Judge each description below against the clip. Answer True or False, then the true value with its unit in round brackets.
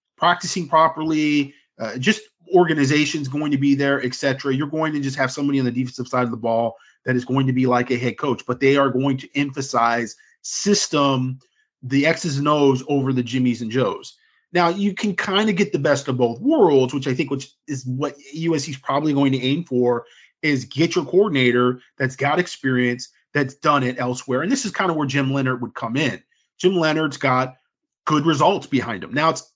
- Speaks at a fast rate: True (210 wpm)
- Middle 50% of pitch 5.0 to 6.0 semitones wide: False (3.8 semitones)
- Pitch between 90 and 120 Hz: False (140 Hz)